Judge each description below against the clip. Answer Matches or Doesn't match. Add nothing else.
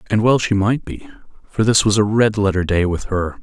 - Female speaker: Doesn't match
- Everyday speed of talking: Doesn't match